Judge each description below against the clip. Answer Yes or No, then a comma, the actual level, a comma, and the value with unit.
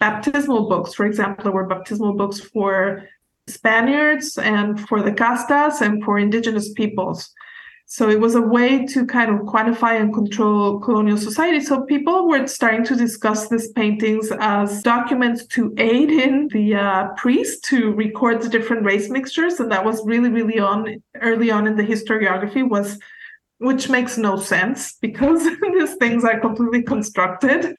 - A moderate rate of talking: Yes, average, 160 wpm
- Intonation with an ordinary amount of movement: Yes, average, 3.8 semitones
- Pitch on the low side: No, high, 230 Hz